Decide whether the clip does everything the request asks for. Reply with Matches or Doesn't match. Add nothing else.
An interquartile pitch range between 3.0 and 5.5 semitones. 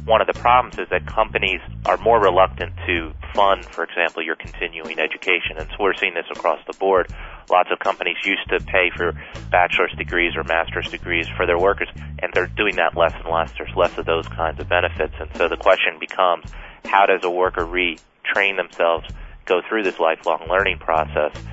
Doesn't match